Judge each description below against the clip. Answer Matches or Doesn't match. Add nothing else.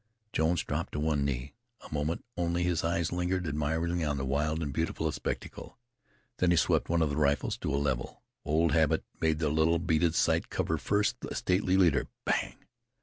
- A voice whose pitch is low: Matches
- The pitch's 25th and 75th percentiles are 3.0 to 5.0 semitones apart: Doesn't match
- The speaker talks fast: Doesn't match